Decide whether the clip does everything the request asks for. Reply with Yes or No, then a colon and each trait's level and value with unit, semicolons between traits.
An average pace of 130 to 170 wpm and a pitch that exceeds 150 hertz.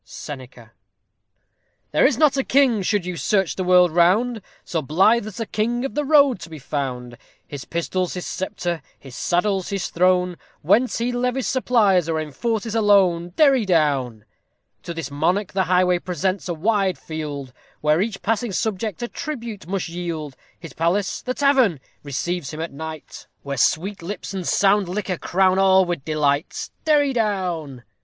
Yes: average, 165 wpm; medium, 185 Hz